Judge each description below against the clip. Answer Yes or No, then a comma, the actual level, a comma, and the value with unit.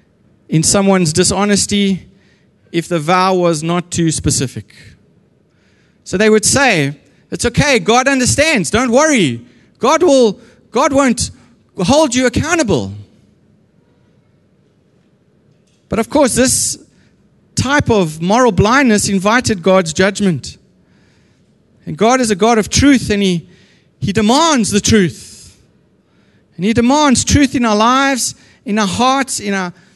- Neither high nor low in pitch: No, high, 205 Hz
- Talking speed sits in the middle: No, slow, 125 wpm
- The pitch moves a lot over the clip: Yes, wide, 5.8 semitones